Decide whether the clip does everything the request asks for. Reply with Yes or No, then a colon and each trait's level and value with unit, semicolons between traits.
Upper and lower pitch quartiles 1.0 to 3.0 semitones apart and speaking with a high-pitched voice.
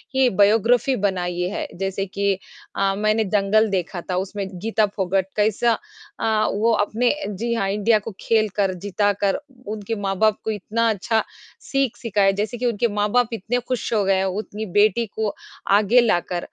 Yes: narrow, 2.5 semitones; high, 210 Hz